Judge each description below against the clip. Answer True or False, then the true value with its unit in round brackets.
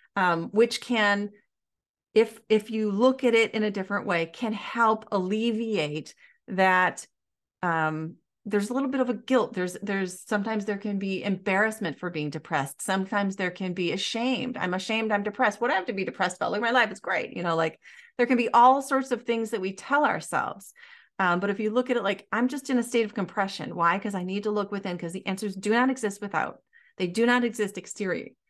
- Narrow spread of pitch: False (3.8 semitones)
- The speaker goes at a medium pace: False (220 wpm)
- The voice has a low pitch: False (210 Hz)